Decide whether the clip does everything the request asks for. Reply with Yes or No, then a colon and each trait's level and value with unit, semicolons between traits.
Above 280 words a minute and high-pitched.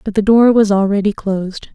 No: fast, 205 wpm; high, 205 Hz